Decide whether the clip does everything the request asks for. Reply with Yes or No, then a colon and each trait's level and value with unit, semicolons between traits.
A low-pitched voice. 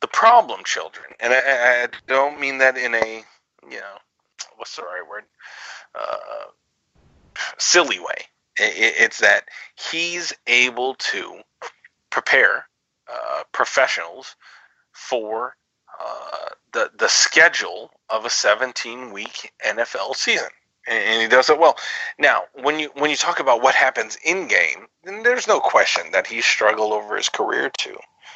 No: medium, 145 Hz